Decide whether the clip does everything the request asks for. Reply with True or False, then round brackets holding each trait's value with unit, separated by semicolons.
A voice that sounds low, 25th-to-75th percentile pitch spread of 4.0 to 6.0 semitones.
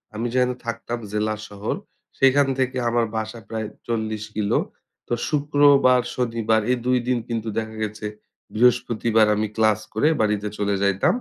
False (115 Hz; 2.7 semitones)